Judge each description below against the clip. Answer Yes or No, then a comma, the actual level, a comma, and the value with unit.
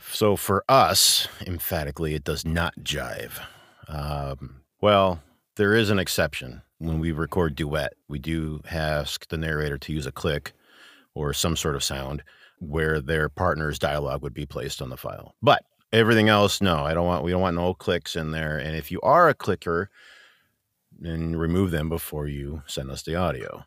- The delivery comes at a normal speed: Yes, average, 180 wpm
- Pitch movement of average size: Yes, average, 3.1 semitones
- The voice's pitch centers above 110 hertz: No, very low, 80 Hz